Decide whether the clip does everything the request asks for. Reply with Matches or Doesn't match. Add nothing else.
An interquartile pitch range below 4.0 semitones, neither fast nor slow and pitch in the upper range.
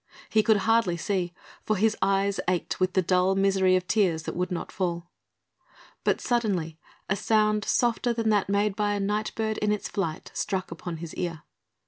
Matches